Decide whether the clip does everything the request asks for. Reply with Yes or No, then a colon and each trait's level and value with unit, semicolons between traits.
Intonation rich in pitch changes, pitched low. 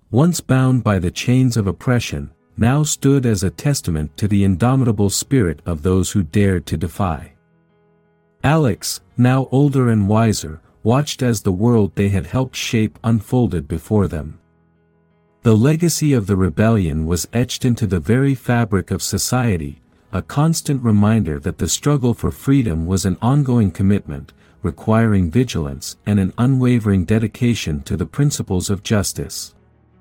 Yes: wide, 6.1 semitones; low, 105 Hz